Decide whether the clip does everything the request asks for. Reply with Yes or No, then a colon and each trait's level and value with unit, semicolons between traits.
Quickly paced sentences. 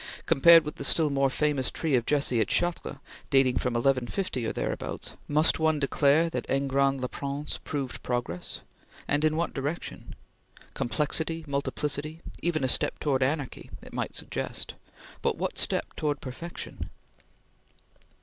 No: average, 145 wpm